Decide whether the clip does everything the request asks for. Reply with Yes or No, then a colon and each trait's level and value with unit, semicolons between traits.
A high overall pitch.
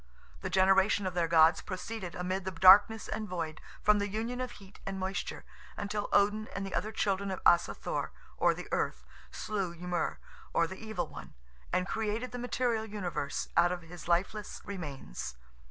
Yes: high, 195 Hz